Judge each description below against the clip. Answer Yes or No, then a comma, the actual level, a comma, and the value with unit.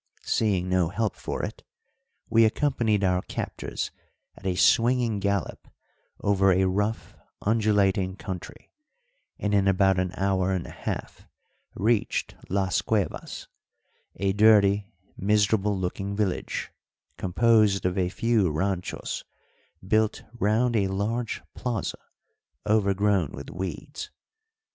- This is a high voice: No, low, 100 Hz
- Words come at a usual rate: No, slow, 115 wpm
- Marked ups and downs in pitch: No, narrow, 2.5 semitones